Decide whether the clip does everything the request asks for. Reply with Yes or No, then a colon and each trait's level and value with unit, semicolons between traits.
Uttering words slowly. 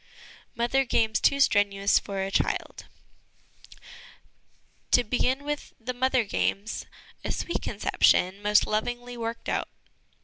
Yes: slow, 125 wpm